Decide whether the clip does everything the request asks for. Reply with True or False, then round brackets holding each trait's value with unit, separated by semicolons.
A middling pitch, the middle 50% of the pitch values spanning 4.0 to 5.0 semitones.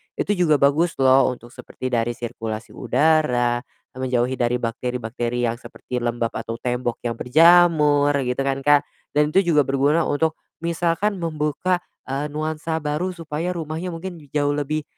True (145 Hz; 4.6 semitones)